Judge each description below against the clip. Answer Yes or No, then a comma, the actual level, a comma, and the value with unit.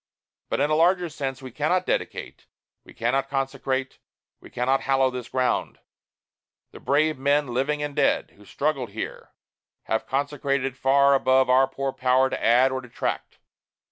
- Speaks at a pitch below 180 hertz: Yes, low, 135 Hz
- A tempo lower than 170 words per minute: Yes, average, 160 wpm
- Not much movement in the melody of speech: Yes, narrow, 1.6 semitones